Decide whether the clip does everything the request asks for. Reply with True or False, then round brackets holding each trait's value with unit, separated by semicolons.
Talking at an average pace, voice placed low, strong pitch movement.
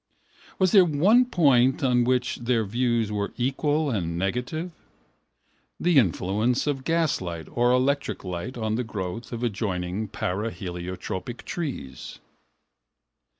False (115 wpm; 120 Hz; 6.0 semitones)